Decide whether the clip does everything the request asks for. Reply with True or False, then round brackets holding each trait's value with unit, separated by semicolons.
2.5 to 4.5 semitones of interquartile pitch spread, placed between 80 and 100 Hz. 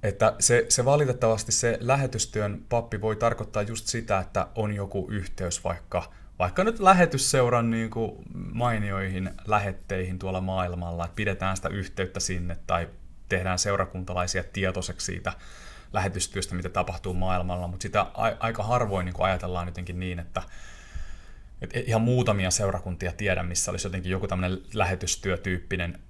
True (3.2 semitones; 95 Hz)